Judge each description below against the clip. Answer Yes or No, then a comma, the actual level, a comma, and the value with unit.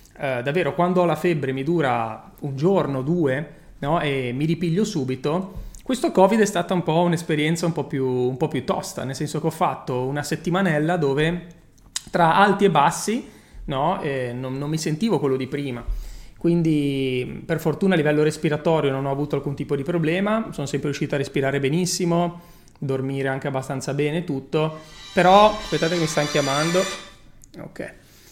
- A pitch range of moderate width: Yes, average, 3.9 semitones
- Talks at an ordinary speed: No, fast, 175 wpm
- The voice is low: No, medium, 155 Hz